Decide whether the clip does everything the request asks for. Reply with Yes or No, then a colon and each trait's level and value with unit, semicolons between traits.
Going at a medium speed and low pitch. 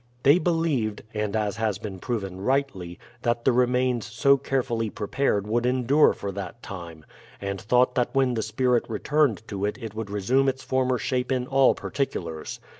Yes: average, 175 wpm; low, 120 Hz